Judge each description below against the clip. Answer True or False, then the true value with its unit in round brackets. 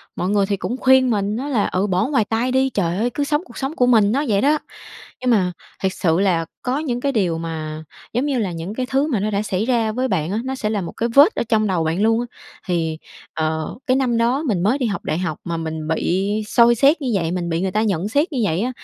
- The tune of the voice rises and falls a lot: True (6.0 semitones)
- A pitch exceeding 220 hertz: False (215 Hz)